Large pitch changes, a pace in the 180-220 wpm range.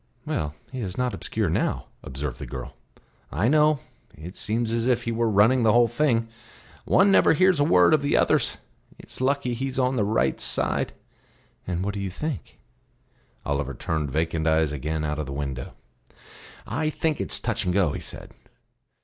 Yes: wide, 8.5 semitones; average, 185 wpm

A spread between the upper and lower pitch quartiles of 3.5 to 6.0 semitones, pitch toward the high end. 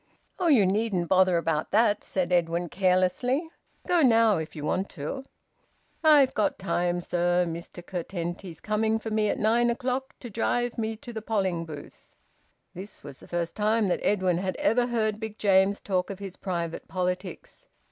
Yes: average, 4.2 semitones; high, 195 Hz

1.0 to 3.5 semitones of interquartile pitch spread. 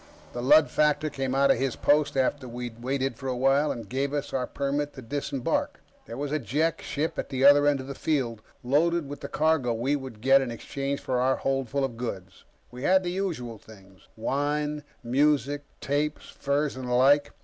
Yes: average, 2.7 semitones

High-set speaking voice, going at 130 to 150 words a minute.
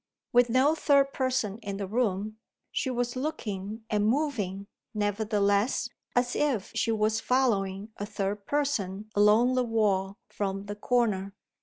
Yes: high, 215 Hz; average, 140 wpm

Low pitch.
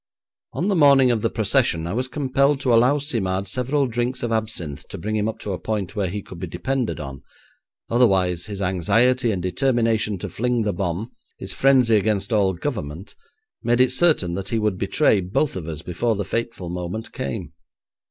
Yes: low, 110 Hz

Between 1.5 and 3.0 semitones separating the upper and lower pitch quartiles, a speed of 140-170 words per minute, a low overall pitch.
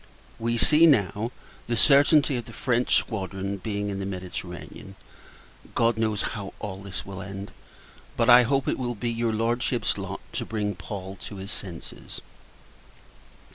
No: average, 3.4 semitones; average, 155 wpm; low, 105 Hz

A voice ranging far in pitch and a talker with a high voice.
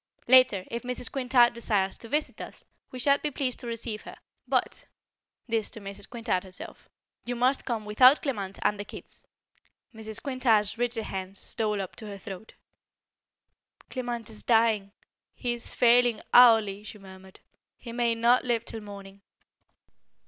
No: average, 3.2 semitones; high, 230 Hz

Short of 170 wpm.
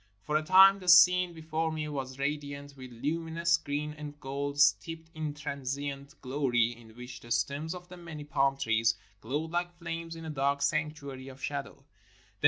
No: average, 180 wpm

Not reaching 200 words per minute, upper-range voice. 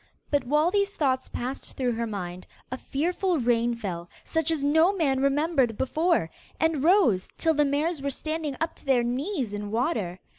Yes: average, 180 wpm; very high, 275 Hz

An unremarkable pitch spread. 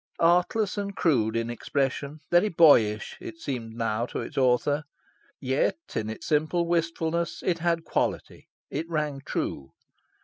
No: wide, 5.9 semitones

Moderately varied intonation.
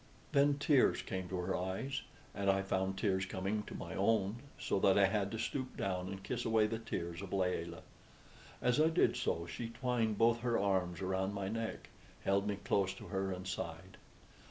Yes: average, 3.2 semitones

